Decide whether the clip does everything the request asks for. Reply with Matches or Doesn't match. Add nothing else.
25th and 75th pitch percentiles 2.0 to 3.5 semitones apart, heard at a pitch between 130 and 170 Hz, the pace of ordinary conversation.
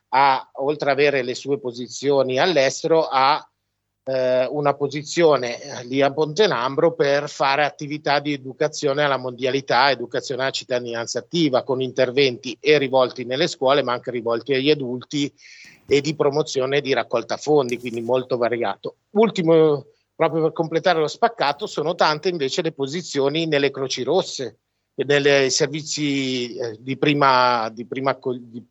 Matches